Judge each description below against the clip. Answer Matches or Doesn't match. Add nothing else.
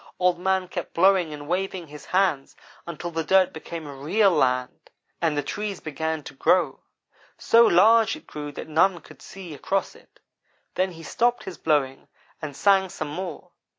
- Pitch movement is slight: Doesn't match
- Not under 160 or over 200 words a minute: Matches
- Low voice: Doesn't match